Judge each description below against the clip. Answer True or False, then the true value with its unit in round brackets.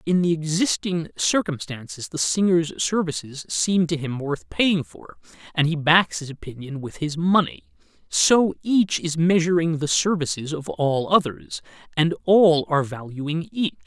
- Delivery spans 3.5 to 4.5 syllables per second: True (4.3 syllables/s)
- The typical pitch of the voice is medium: True (155 Hz)